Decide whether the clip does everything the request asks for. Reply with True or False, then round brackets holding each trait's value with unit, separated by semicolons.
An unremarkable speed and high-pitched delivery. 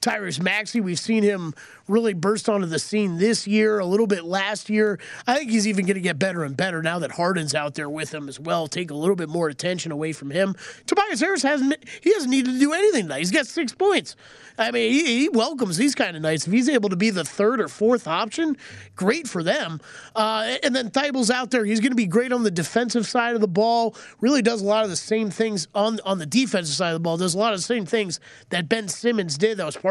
False (260 wpm; 215 Hz)